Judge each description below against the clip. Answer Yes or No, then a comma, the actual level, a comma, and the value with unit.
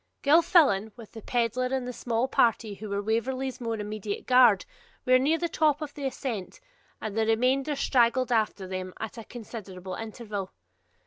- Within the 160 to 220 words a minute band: Yes, average, 170 wpm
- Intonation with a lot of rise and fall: No, average, 3.4 semitones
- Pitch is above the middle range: Yes, high, 230 Hz